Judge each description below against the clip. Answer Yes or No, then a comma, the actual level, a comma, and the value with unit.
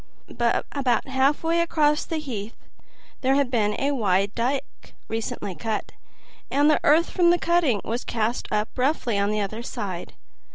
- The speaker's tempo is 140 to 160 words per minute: Yes, average, 155 wpm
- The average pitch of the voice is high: Yes, very high, 250 Hz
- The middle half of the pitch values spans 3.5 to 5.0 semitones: No, wide, 5.5 semitones